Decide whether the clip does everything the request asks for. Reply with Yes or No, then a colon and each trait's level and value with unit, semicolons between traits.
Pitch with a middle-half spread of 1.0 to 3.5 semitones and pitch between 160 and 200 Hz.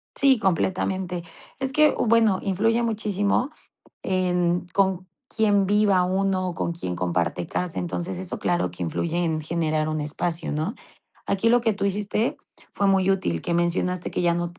Yes: average, 3.1 semitones; medium, 185 Hz